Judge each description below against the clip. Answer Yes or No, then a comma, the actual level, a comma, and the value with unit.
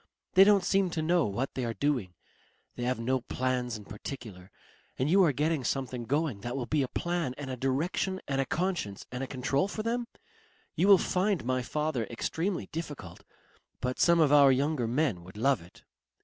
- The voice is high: No, low, 135 Hz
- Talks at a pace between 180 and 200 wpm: Yes, average, 195 wpm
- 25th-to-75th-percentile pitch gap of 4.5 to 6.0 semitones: Yes, average, 5.2 semitones